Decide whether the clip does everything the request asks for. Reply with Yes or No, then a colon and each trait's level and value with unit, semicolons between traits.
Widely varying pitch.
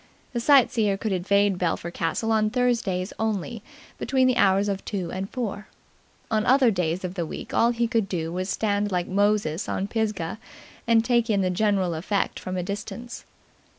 No: average, 3.5 semitones